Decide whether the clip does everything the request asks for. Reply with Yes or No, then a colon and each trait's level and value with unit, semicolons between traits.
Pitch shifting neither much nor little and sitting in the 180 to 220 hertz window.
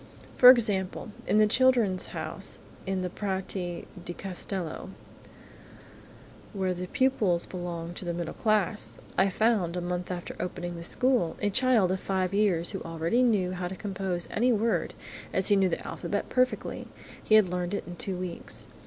Yes: average, 3.3 semitones; high, 190 Hz